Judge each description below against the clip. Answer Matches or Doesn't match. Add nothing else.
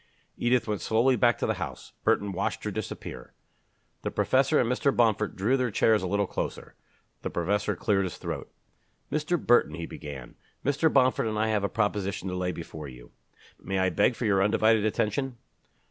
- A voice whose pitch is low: Matches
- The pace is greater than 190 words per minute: Doesn't match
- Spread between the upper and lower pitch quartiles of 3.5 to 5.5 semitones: Matches